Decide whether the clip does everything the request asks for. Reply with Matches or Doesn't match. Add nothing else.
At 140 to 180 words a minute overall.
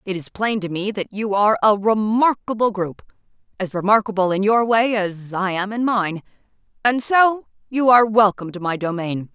Matches